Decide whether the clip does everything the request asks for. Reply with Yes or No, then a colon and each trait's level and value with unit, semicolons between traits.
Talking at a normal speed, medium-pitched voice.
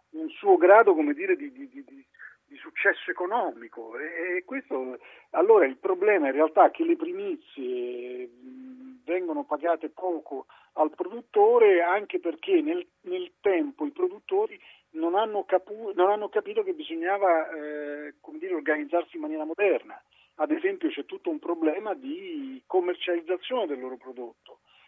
No: average, 150 wpm; very high, 275 Hz